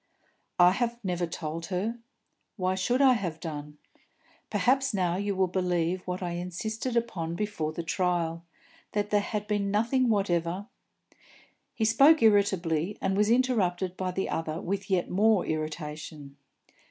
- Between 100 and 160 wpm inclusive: Yes, average, 150 wpm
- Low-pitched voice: No, medium, 185 Hz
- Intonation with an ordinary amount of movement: Yes, average, 3.8 semitones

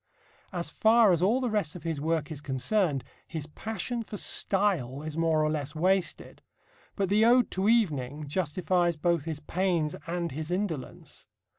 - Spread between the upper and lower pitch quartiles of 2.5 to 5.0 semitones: Yes, average, 4.4 semitones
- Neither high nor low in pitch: Yes, medium, 170 Hz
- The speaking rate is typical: Yes, average, 165 wpm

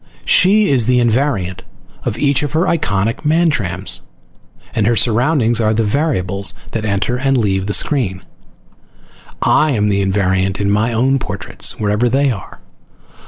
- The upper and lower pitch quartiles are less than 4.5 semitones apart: No, wide, 5.5 semitones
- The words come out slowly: No, average, 150 wpm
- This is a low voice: Yes, low, 115 Hz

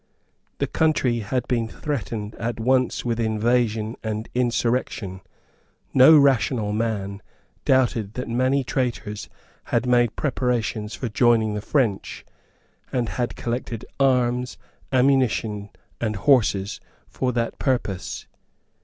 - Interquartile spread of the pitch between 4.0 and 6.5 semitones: No, average, 2.8 semitones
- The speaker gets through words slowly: Yes, slow, 110 wpm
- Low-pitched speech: Yes, low, 120 Hz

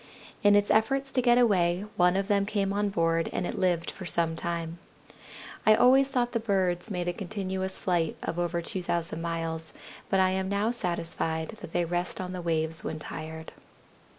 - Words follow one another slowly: No, average, 185 wpm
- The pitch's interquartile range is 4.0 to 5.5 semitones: No, average, 3.4 semitones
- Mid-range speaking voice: Yes, medium, 180 Hz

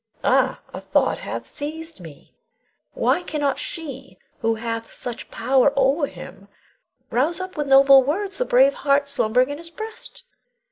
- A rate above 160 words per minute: No, average, 150 wpm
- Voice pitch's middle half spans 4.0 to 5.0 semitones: Yes, average, 4.3 semitones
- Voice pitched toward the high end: Yes, very high, 275 Hz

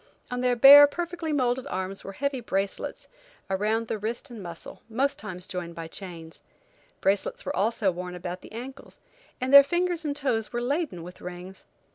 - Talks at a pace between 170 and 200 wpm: Yes, average, 175 wpm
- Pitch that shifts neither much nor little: No, wide, 6.8 semitones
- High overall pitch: Yes, high, 225 Hz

